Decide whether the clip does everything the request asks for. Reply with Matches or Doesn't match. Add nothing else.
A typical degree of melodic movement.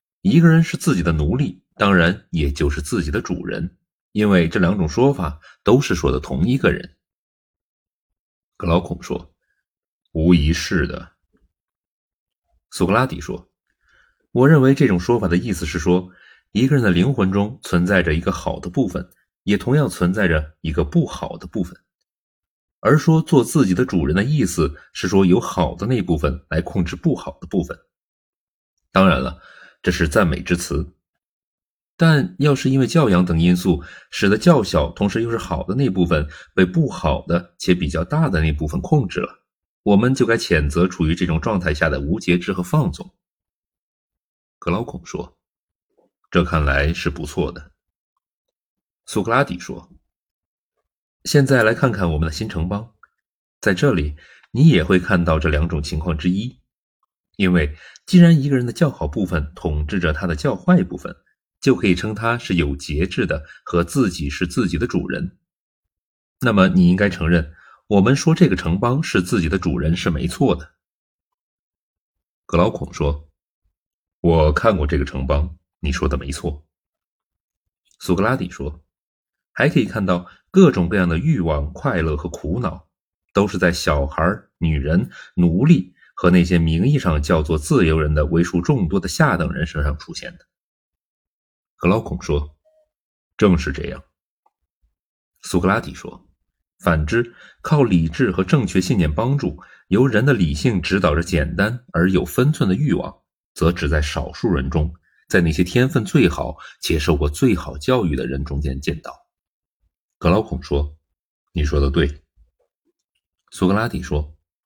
Matches